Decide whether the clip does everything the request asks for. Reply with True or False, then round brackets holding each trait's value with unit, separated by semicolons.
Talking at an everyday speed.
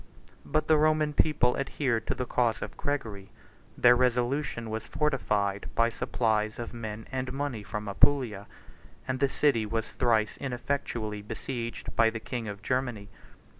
True (155 wpm)